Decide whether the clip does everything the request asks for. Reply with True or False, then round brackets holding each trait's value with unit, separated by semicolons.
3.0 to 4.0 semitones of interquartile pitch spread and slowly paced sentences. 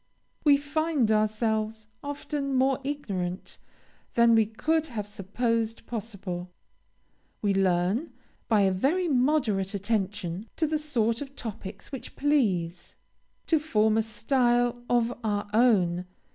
False (5.1 semitones; 120 wpm)